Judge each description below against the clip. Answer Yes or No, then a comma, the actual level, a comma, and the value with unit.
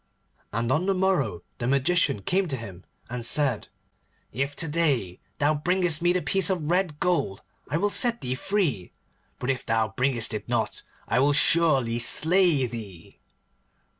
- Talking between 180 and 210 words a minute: No, average, 165 wpm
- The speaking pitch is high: No, medium, 140 Hz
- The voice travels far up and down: Yes, wide, 7.0 semitones